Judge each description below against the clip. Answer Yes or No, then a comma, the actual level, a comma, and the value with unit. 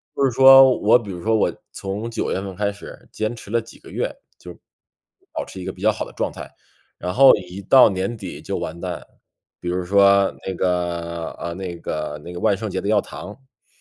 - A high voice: No, low, 100 Hz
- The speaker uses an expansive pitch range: No, average, 3.8 semitones